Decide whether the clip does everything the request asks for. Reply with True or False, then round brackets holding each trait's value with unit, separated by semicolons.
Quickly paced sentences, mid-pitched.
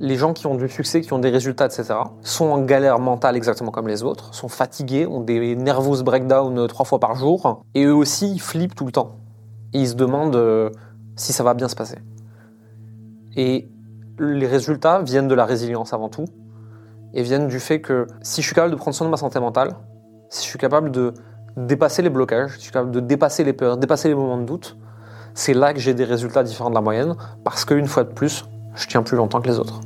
False (230 wpm; 125 Hz)